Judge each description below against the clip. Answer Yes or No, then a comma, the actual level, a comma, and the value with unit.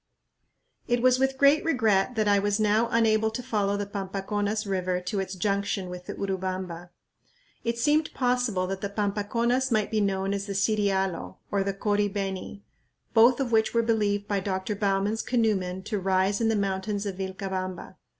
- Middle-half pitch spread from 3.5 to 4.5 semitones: No, narrow, 2.5 semitones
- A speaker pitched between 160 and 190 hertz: No, high, 205 Hz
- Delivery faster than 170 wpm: Yes, average, 180 wpm